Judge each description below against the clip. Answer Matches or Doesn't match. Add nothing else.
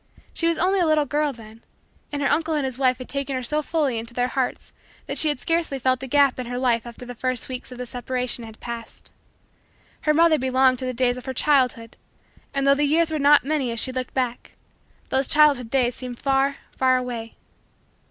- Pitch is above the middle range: Matches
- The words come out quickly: Matches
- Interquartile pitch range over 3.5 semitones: Doesn't match